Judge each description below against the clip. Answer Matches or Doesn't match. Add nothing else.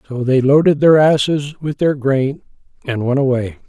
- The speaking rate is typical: Matches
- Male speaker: Matches